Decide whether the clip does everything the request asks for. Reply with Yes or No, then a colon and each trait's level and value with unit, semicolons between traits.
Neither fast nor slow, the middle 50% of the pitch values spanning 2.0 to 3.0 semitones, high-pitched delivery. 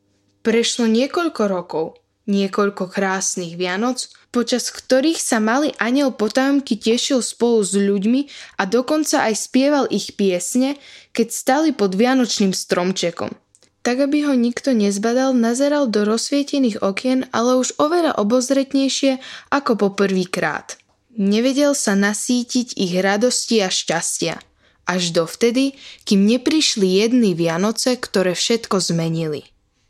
No: average, 120 wpm; average, 4.8 semitones; high, 230 Hz